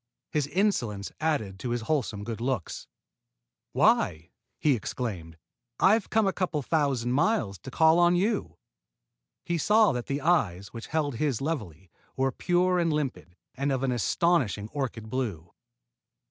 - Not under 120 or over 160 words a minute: Yes, average, 150 wpm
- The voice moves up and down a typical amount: No, wide, 7.1 semitones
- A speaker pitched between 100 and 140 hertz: Yes, low, 135 Hz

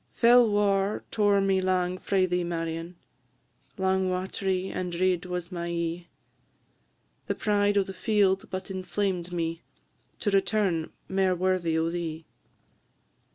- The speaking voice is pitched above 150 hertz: Yes, medium, 185 Hz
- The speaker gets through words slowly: Yes, slow, 130 wpm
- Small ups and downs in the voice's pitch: Yes, narrow, 2.1 semitones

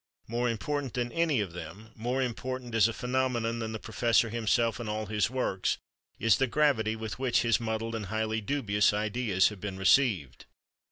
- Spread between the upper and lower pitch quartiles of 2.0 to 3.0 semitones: Yes, average, 2.7 semitones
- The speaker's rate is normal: Yes, average, 180 wpm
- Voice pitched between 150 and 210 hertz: No, low, 115 Hz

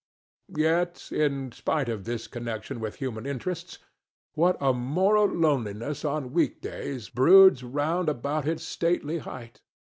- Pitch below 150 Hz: Yes, medium, 140 Hz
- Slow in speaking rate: Yes, slow, 130 wpm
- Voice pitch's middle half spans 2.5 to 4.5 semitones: No, average, 5.2 semitones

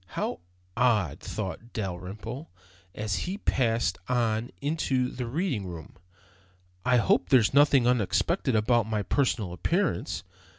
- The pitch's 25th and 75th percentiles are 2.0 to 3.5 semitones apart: No, average, 4.1 semitones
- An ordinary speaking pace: No, slow, 120 wpm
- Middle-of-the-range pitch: No, low, 115 Hz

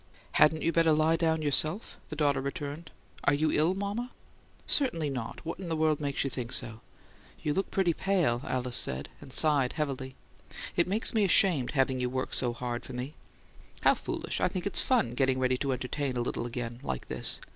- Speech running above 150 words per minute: Yes, average, 200 wpm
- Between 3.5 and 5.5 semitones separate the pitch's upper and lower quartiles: Yes, average, 4.3 semitones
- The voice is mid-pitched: Yes, medium, 145 Hz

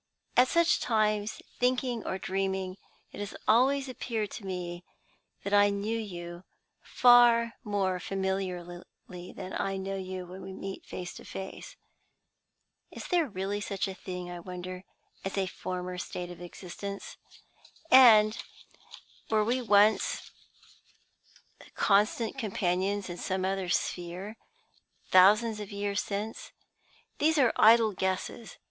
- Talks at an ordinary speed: No, slow, 130 wpm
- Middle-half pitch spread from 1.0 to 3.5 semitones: Yes, average, 3.0 semitones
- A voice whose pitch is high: Yes, high, 195 Hz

